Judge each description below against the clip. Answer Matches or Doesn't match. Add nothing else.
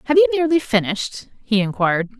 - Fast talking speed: Doesn't match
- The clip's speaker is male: Doesn't match